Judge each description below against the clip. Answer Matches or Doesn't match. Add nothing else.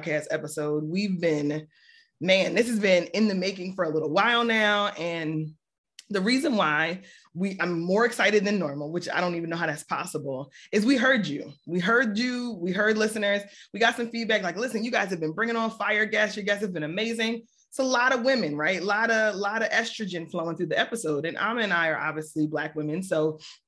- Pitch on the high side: Matches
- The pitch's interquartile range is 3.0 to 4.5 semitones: Doesn't match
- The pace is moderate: Doesn't match